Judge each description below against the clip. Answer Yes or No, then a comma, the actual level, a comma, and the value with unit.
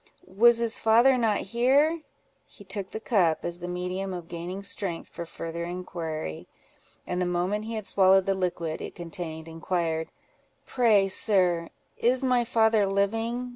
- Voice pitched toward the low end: No, high, 190 Hz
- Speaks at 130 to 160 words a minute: Yes, average, 150 wpm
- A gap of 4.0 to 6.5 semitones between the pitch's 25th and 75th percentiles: Yes, average, 4.5 semitones